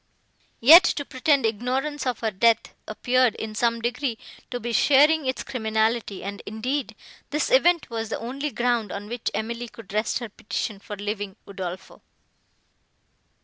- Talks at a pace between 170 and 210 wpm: No, average, 150 wpm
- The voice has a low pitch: No, high, 235 Hz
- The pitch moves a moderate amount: Yes, average, 3.3 semitones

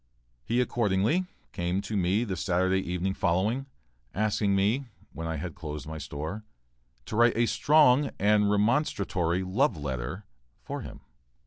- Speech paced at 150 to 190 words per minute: No, average, 140 wpm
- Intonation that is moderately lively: Yes, average, 4.8 semitones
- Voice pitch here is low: Yes, low, 100 Hz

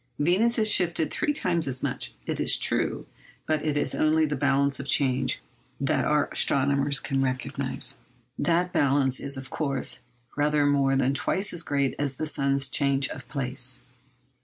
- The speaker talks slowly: No, average, 165 wpm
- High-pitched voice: No, medium, 140 Hz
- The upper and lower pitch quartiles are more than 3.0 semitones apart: No, narrow, 2.5 semitones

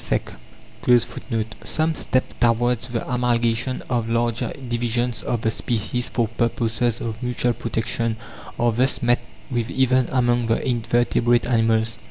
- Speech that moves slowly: Yes, slow, 130 wpm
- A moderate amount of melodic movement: No, narrow, 1.2 semitones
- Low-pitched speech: Yes, low, 120 Hz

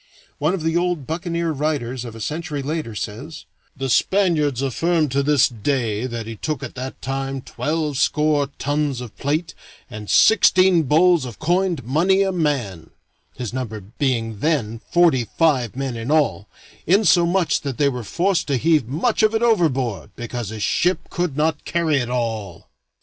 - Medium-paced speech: Yes, average, 165 wpm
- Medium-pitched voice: Yes, medium, 145 Hz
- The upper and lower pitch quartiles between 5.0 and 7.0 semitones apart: Yes, wide, 5.4 semitones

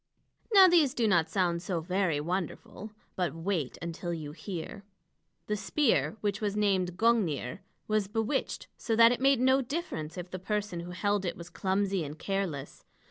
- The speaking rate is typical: Yes, average, 170 wpm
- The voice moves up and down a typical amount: Yes, average, 4.2 semitones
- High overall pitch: Yes, high, 195 Hz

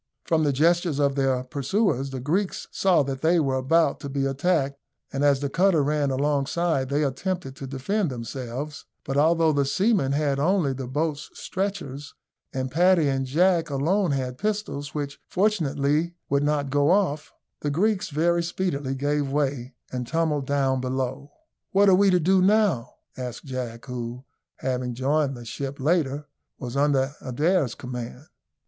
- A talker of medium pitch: Yes, medium, 145 Hz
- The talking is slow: No, average, 160 wpm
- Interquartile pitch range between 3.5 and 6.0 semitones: Yes, average, 4.0 semitones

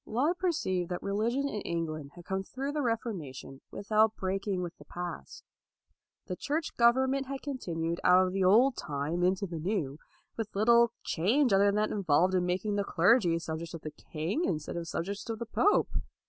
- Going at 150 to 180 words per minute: No, average, 190 wpm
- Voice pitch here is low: No, high, 195 Hz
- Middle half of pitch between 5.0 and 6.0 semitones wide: Yes, wide, 5.6 semitones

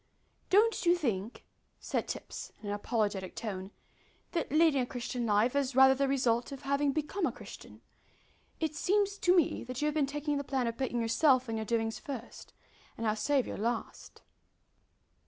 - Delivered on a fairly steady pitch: No, average, 4.5 semitones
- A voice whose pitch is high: Yes, very high, 265 Hz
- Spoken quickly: No, average, 175 wpm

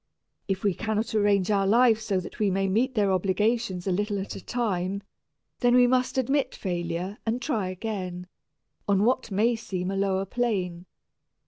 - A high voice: Yes, high, 200 Hz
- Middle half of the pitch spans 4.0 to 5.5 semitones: No, average, 3.4 semitones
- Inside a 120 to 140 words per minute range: No, average, 175 wpm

